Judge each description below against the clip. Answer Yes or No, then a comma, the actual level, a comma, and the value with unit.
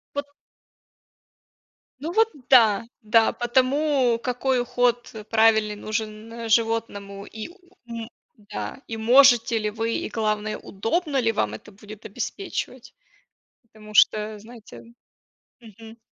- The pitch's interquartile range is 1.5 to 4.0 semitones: Yes, narrow, 2.4 semitones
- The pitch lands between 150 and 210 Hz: No, high, 225 Hz